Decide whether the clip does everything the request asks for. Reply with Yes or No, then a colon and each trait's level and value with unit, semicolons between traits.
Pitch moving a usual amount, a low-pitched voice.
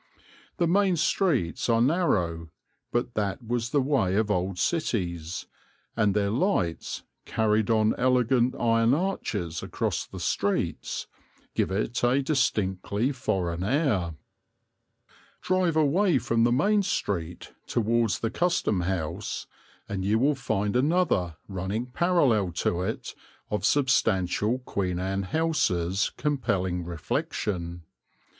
No: wide, 6.4 semitones; low, 110 Hz